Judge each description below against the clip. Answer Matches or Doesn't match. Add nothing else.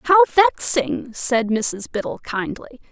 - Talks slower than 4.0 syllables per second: Matches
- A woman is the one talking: Matches